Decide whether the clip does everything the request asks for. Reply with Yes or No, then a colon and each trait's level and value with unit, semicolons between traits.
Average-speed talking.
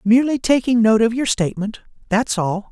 Yes: average, 175 wpm